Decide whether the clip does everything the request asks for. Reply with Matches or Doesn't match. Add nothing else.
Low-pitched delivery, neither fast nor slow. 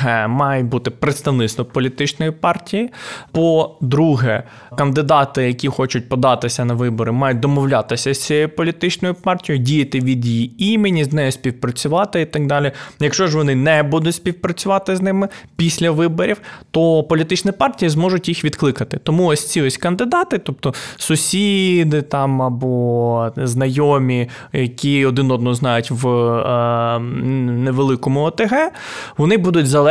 Doesn't match